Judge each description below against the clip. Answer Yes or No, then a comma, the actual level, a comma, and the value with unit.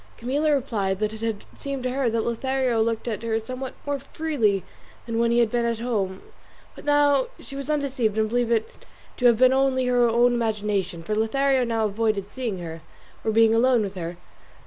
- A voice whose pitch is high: Yes, high, 230 Hz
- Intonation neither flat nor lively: Yes, average, 3.1 semitones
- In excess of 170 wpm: Yes, fast, 205 wpm